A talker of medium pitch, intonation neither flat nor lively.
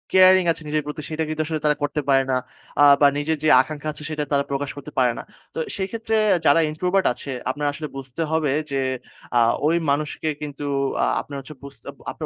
No: medium, 150 Hz; narrow, 2.1 semitones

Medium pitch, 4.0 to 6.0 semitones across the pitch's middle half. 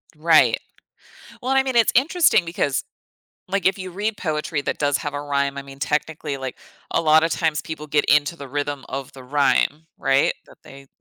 No: medium, 150 Hz; average, 3.4 semitones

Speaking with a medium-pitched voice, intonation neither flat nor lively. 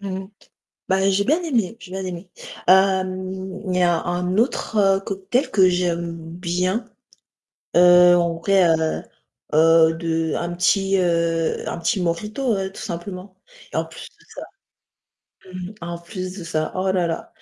No: medium, 180 Hz; narrow, 2.1 semitones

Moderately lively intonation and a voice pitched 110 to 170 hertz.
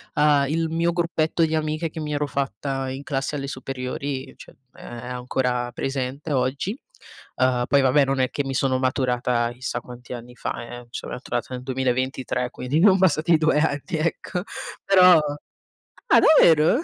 Yes: average, 3.6 semitones; low, 135 Hz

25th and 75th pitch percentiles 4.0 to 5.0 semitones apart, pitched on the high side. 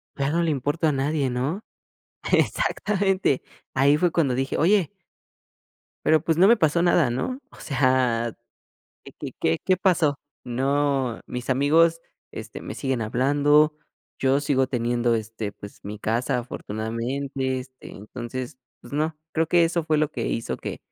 No: average, 4.3 semitones; medium, 140 Hz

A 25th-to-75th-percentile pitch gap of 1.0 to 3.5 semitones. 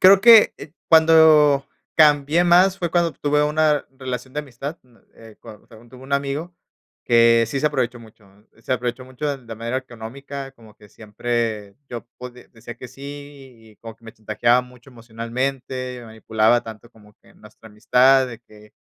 No: average, 3.9 semitones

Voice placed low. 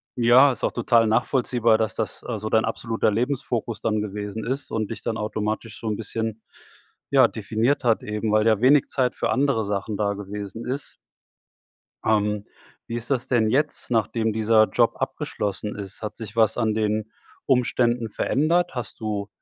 Yes: low, 110 Hz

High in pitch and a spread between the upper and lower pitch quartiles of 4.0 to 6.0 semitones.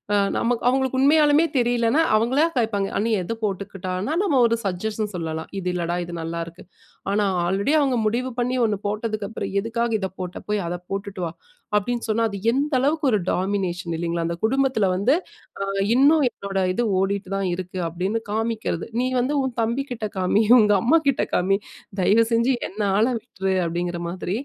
Yes: high, 210 Hz; average, 4.6 semitones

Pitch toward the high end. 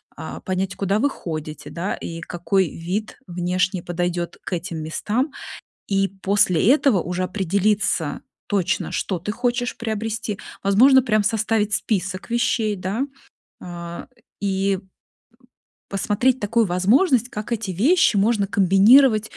Yes: high, 200 Hz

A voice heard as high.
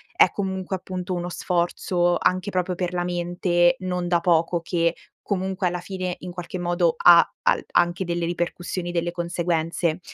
No: medium, 175 Hz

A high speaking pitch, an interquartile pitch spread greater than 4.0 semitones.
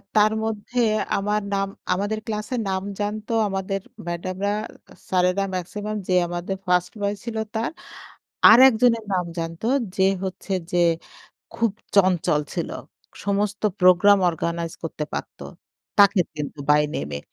No: high, 195 Hz; average, 2.9 semitones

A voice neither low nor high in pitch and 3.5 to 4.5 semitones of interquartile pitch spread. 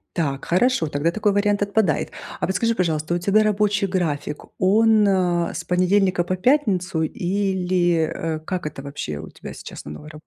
Yes: medium, 180 Hz; average, 4.1 semitones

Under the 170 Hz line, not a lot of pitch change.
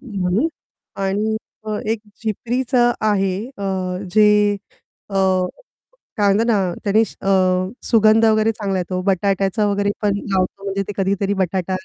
No: high, 200 Hz; narrow, 2.2 semitones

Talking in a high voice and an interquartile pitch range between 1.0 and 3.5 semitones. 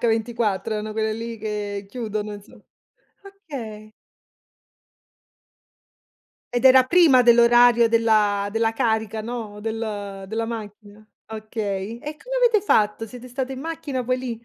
Yes: high, 225 Hz; narrow, 2.6 semitones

